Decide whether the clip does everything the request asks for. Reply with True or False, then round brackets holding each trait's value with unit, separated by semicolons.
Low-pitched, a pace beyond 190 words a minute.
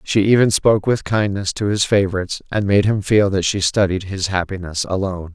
True (100 Hz; 200 wpm)